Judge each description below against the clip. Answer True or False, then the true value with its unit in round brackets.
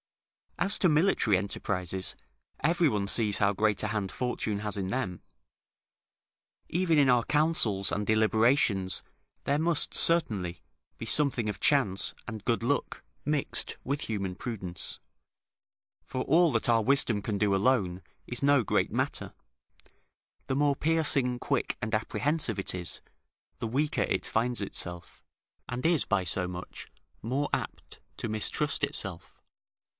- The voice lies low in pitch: True (115 Hz)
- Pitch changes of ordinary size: False (6.0 semitones)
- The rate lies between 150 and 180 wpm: False (140 wpm)